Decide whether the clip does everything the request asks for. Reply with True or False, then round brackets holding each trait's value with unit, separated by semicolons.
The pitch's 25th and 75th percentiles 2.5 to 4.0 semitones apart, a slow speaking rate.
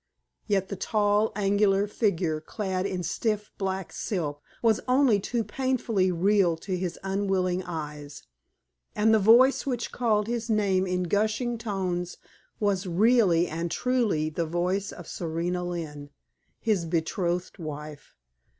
True (3.6 semitones; 130 wpm)